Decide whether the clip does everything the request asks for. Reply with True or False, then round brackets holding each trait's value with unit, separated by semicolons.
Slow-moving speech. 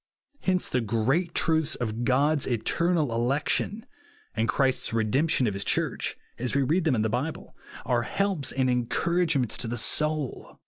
False (155 wpm)